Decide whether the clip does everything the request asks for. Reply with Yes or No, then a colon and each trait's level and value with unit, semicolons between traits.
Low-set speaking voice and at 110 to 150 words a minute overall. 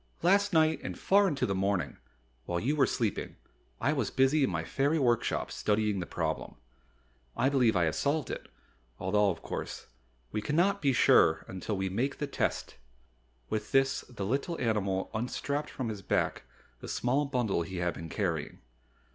No: low, 115 Hz; average, 175 wpm